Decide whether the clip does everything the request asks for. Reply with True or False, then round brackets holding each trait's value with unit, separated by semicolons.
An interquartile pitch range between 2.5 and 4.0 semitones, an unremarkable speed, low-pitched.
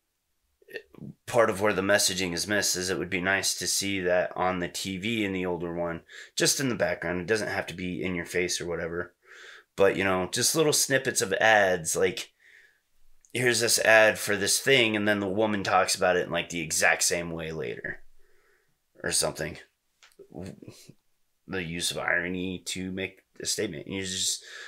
True (3.0 semitones; 185 wpm; 95 Hz)